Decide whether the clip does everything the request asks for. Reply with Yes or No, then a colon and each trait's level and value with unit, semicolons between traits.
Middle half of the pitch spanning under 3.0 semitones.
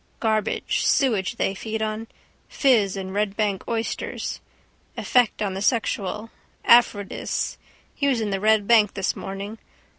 Yes: narrow, 2.4 semitones